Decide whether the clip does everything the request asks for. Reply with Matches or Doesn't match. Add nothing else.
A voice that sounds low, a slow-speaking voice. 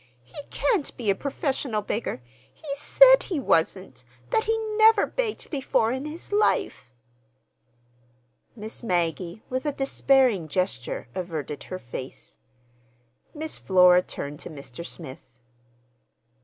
Doesn't match